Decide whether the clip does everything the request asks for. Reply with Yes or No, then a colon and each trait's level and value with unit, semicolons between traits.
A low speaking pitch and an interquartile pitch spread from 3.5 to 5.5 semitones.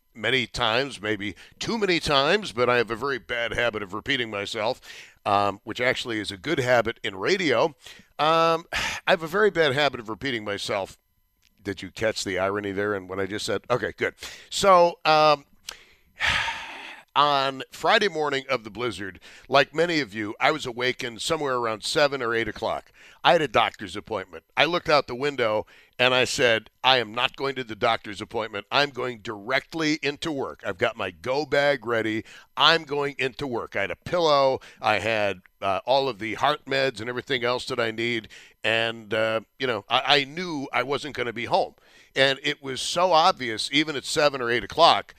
Yes: low, 125 Hz; average, 4.5 semitones